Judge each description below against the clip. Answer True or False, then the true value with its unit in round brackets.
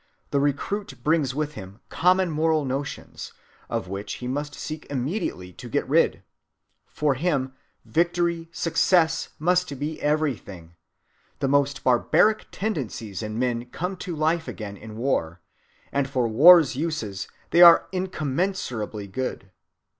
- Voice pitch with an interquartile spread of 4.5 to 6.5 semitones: True (5.5 semitones)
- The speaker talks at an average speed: False (130 wpm)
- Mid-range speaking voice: True (145 Hz)